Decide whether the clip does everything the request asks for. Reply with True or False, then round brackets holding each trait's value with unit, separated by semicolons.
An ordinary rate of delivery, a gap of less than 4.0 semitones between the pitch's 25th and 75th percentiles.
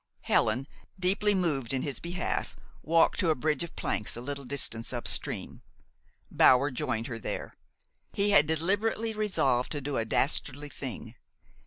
False (155 wpm; 5.6 semitones)